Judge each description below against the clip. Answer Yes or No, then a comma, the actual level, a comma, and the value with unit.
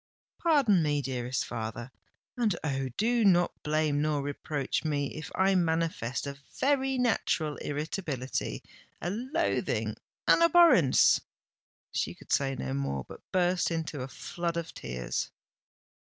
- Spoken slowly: Yes, slow, 120 wpm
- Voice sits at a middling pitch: Yes, medium, 155 Hz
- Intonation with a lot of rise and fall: Yes, wide, 6.2 semitones